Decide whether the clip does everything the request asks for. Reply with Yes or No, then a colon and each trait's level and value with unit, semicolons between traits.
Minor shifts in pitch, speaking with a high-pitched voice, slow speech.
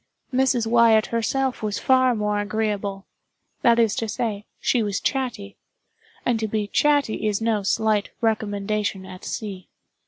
No: narrow, 2.2 semitones; high, 220 Hz; average, 145 wpm